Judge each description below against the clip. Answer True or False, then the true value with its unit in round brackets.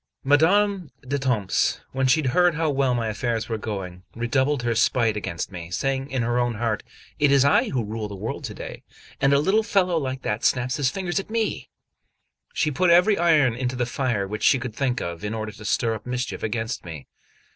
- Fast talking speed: True (210 wpm)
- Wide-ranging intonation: False (4.6 semitones)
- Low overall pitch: True (125 Hz)